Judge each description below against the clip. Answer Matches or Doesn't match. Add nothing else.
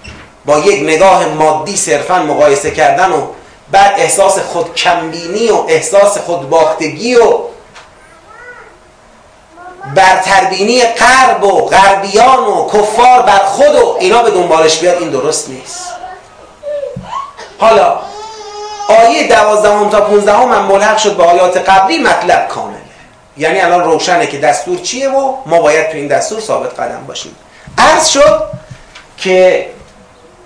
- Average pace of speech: Matches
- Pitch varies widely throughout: Matches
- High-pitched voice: Matches